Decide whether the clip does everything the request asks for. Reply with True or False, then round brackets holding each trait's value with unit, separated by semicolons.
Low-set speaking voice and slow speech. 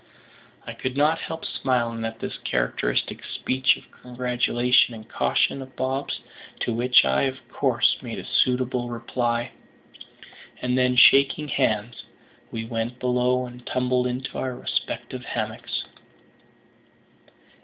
True (125 Hz; 125 wpm)